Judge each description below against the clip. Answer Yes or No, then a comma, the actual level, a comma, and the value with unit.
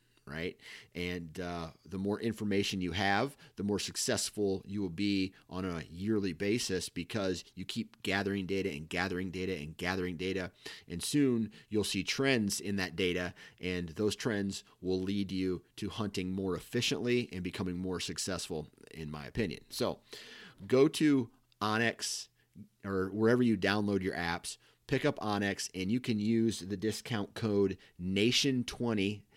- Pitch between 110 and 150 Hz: No, low, 100 Hz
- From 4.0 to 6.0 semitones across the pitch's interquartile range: No, average, 2.9 semitones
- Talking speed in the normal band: Yes, average, 155 wpm